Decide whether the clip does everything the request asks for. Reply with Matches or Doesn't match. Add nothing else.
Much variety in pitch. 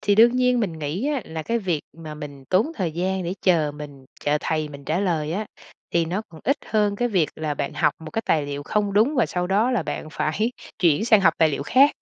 Matches